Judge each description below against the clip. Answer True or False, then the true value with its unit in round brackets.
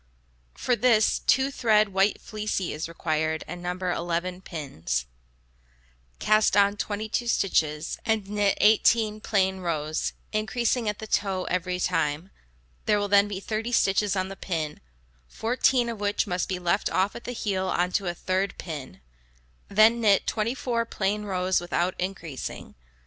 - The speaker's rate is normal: True (150 wpm)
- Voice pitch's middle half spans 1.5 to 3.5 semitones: True (3.2 semitones)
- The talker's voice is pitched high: True (195 Hz)